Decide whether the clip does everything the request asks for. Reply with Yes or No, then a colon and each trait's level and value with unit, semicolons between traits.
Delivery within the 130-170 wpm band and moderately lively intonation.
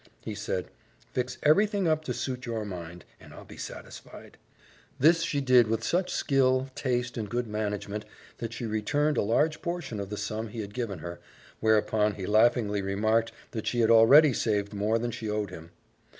No: average, 185 wpm; average, 3.5 semitones